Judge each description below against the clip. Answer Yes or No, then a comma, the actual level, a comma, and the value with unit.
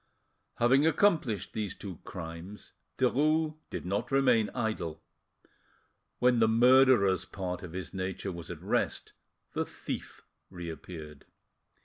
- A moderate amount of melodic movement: No, wide, 6.0 semitones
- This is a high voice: No, low, 105 Hz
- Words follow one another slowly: Yes, slow, 115 wpm